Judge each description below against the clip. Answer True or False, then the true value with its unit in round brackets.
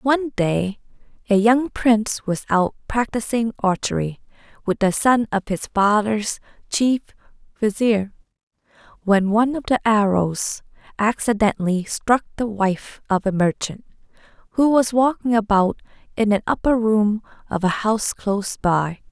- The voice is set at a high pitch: True (215 Hz)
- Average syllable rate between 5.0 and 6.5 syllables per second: False (4.4 syllables/s)